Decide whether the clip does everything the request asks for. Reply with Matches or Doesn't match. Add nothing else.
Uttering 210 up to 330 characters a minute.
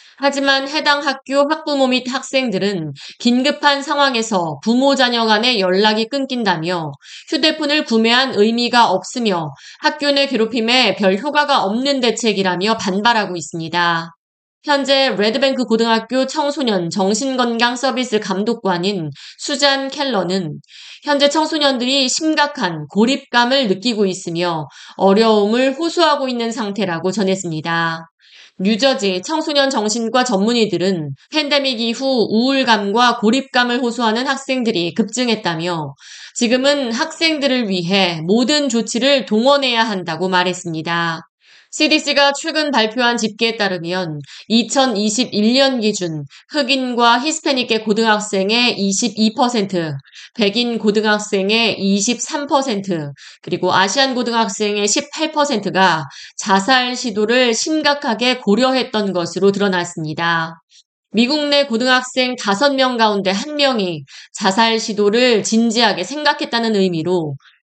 Matches